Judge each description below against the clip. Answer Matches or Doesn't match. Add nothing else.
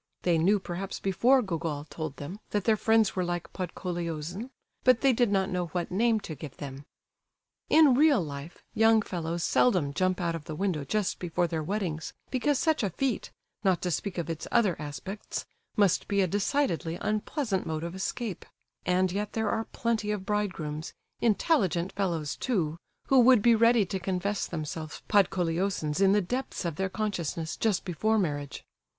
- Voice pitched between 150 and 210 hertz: Matches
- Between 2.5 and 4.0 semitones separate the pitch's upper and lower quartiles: Doesn't match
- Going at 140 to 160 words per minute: Doesn't match